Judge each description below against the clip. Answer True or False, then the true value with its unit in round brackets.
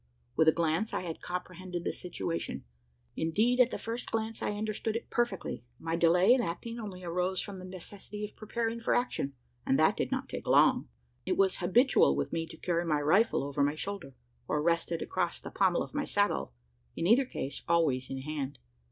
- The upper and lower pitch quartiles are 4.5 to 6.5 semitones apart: True (4.9 semitones)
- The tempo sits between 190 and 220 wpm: True (195 wpm)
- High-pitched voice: False (180 Hz)